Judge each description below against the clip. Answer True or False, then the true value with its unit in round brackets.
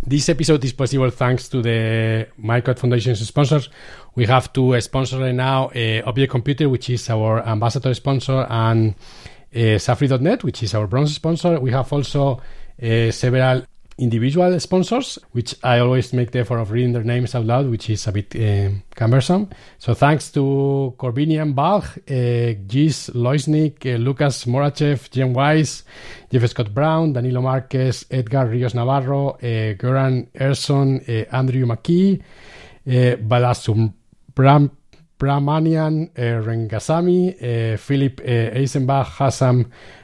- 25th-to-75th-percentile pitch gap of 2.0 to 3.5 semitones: True (3.0 semitones)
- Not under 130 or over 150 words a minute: True (140 wpm)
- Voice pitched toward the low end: True (130 Hz)